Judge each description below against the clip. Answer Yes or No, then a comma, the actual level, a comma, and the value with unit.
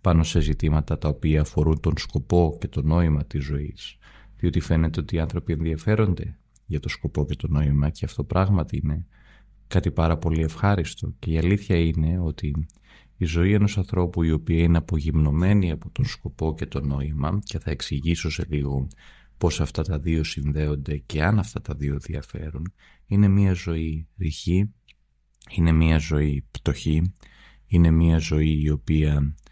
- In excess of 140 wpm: Yes, average, 165 wpm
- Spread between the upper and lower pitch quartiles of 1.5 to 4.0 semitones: Yes, average, 2.9 semitones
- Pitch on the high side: No, very low, 80 Hz